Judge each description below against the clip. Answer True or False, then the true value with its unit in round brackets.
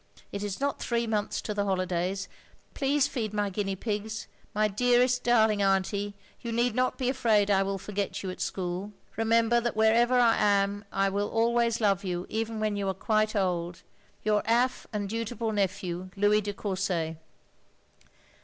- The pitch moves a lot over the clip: False (2.7 semitones)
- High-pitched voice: True (210 Hz)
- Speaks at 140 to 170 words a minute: False (180 wpm)